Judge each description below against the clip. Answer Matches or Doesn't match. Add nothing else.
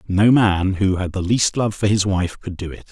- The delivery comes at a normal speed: Doesn't match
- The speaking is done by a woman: Doesn't match